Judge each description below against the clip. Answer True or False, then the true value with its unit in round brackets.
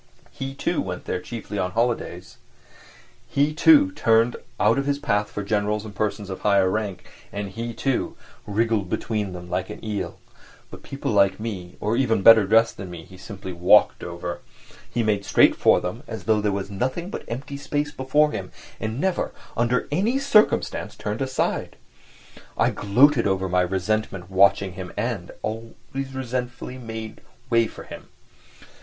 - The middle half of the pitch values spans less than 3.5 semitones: False (4.6 semitones)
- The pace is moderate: True (165 wpm)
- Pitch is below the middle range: True (110 Hz)